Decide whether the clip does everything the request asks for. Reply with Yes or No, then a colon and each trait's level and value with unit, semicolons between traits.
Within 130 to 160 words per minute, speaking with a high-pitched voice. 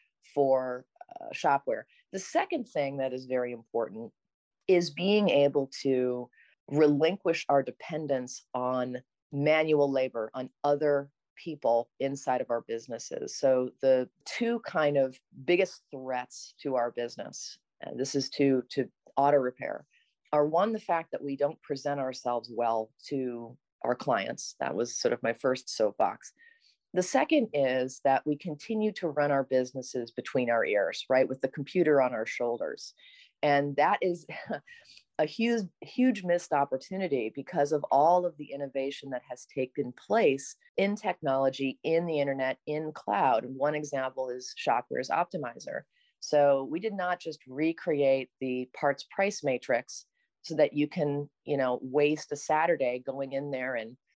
No: average, 150 wpm; medium, 140 Hz